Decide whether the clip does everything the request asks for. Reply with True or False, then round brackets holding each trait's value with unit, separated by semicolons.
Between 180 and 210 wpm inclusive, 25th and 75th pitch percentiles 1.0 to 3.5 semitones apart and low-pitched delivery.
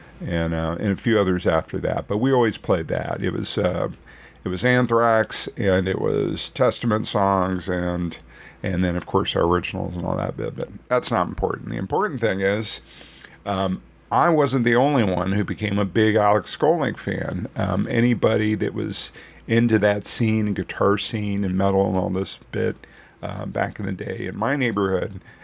True (190 wpm; 3.1 semitones; 100 Hz)